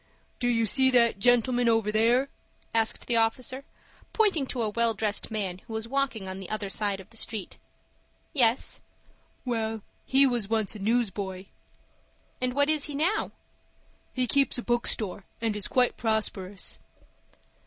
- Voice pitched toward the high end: Yes, high, 230 Hz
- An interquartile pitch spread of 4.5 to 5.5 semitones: No, average, 3.1 semitones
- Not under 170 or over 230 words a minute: No, average, 155 wpm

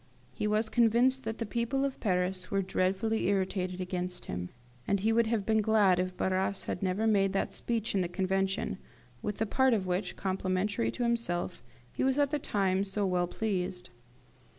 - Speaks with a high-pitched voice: Yes, high, 195 Hz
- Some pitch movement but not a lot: Yes, average, 3.2 semitones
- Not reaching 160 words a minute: No, average, 185 wpm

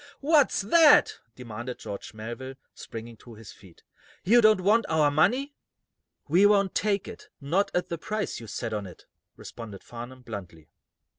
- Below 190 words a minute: Yes, average, 155 wpm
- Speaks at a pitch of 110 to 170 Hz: Yes, medium, 140 Hz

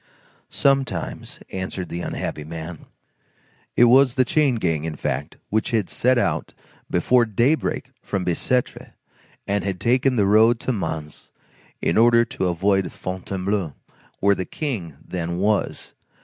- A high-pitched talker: No, low, 100 Hz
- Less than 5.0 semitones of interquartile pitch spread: No, wide, 5.5 semitones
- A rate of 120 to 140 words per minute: Yes, slow, 135 wpm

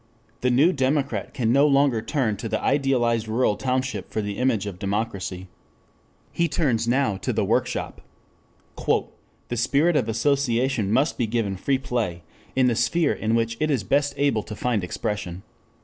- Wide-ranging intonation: No, average, 4.1 semitones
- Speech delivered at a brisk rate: No, average, 165 wpm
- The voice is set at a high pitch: No, low, 120 Hz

